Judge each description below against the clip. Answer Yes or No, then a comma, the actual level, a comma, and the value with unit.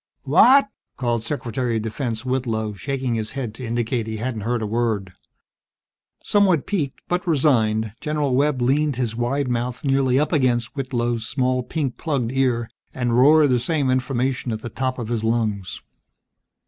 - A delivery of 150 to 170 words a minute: Yes, average, 160 wpm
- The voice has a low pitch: Yes, low, 125 Hz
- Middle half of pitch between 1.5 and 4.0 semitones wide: Yes, average, 3.0 semitones